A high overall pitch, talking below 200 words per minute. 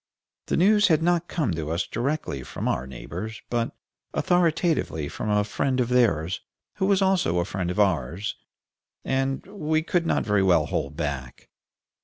No: low, 115 Hz; average, 165 wpm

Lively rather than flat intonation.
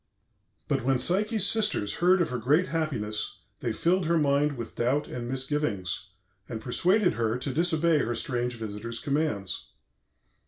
Yes: wide, 6.1 semitones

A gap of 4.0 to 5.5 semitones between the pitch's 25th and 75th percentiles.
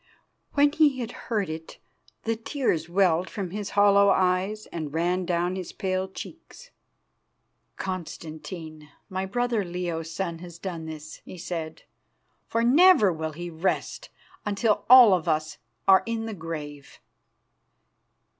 Yes: average, 4.5 semitones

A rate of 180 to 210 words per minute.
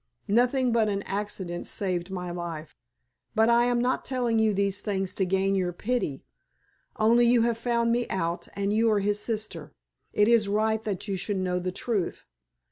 Yes: average, 185 wpm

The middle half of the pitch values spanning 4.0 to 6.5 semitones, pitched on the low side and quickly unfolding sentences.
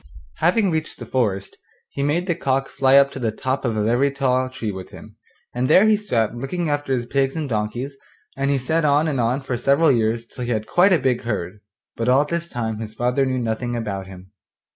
No: average, 3.6 semitones; low, 130 Hz; fast, 230 wpm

